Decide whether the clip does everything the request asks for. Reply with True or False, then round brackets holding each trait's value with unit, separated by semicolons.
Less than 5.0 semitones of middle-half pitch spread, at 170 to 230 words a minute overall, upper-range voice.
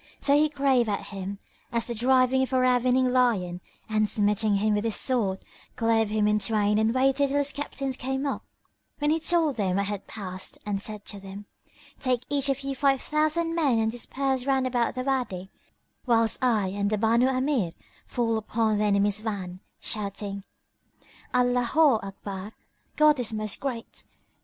True (4.3 semitones; 175 wpm; 230 Hz)